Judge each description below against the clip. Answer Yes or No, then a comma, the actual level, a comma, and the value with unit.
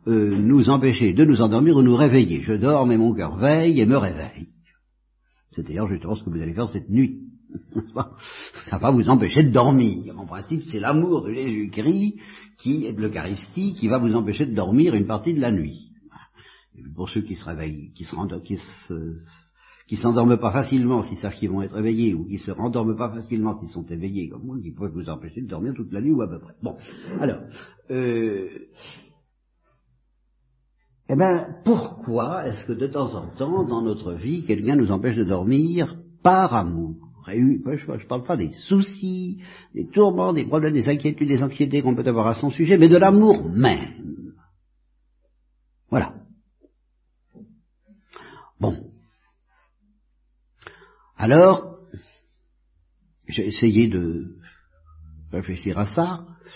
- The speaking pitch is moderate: No, low, 115 Hz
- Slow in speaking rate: No, average, 165 wpm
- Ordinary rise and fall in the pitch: No, wide, 8.2 semitones